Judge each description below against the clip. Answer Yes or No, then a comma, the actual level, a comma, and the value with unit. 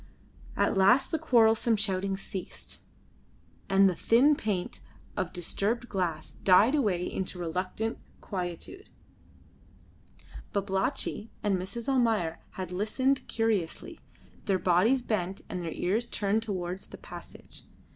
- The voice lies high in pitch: Yes, high, 195 Hz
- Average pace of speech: No, slow, 115 wpm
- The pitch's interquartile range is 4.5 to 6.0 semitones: No, average, 3.8 semitones